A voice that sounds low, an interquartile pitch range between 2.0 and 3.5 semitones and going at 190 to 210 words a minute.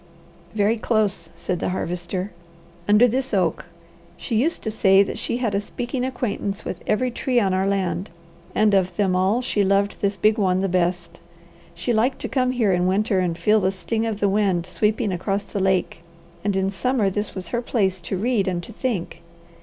No: high, 200 Hz; average, 3.0 semitones; average, 200 wpm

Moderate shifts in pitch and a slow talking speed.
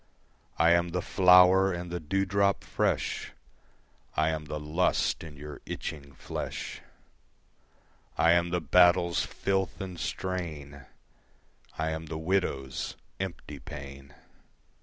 Yes: average, 3.3 semitones; slow, 115 wpm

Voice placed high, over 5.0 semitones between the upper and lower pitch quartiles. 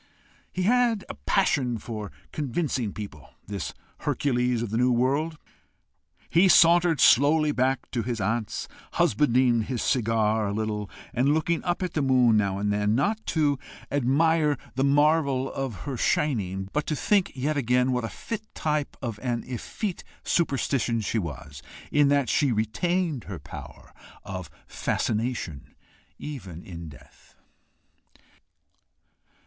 No: low, 130 Hz; wide, 5.6 semitones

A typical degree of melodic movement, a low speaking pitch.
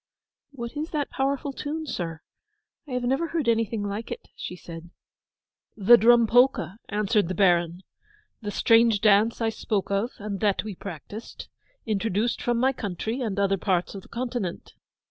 No: average, 3.9 semitones; high, 220 Hz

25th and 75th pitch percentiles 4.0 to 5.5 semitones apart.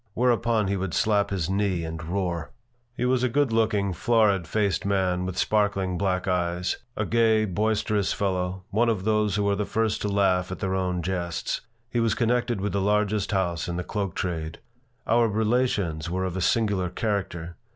No: average, 3.0 semitones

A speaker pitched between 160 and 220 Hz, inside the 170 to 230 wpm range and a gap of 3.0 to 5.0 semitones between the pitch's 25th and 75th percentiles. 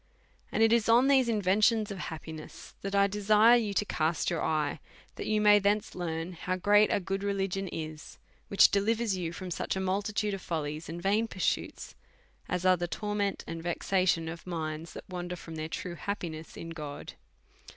Yes: medium, 185 Hz; average, 190 wpm; average, 3.8 semitones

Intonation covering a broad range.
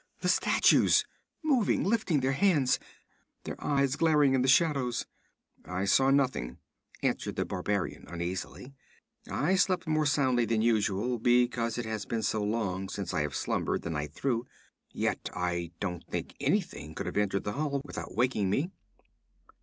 Yes: wide, 6.0 semitones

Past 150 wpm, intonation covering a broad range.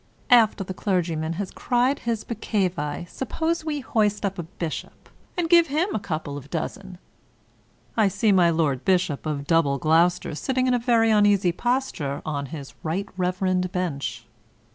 Yes: average, 165 wpm; wide, 6.2 semitones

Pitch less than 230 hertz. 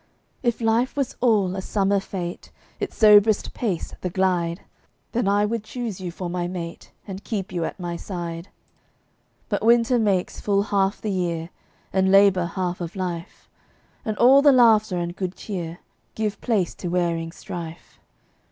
Yes: high, 190 Hz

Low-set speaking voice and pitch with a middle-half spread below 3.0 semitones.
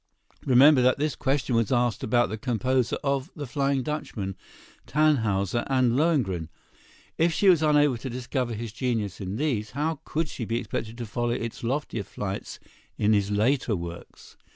No: low, 125 Hz; average, 4.4 semitones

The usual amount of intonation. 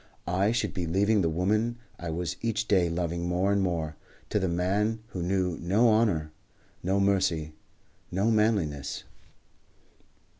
Yes: average, 3.5 semitones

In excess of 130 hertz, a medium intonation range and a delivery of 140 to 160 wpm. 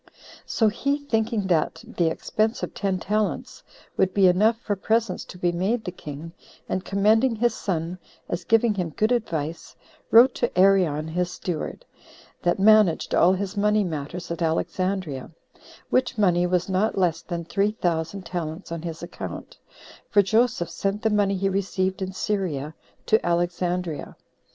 Yes: high, 190 Hz; average, 3.6 semitones; average, 155 wpm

